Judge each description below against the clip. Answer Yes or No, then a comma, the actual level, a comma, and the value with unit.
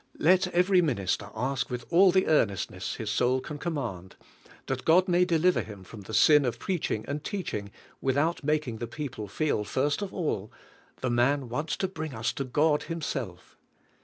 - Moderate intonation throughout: No, wide, 5.9 semitones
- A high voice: No, medium, 140 Hz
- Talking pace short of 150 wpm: No, average, 185 wpm